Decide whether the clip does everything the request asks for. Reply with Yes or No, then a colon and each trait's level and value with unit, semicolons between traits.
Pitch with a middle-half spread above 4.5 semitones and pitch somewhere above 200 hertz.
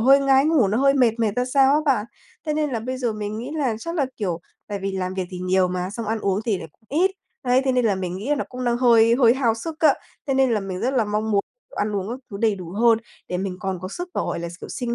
Yes: average, 5.0 semitones; high, 230 Hz